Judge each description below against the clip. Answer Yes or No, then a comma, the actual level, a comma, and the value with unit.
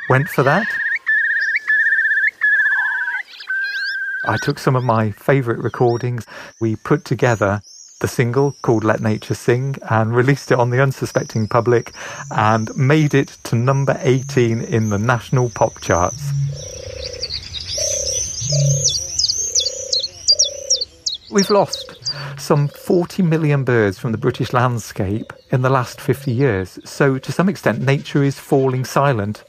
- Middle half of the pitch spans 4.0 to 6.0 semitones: Yes, average, 5.3 semitones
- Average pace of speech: No, slow, 120 wpm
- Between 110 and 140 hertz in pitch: Yes, low, 135 Hz